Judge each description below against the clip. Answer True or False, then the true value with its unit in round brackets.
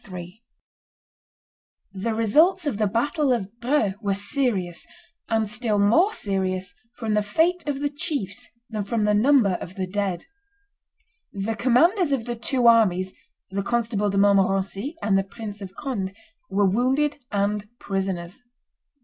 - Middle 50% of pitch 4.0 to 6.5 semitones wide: True (4.4 semitones)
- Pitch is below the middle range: False (210 Hz)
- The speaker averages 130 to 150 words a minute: True (145 wpm)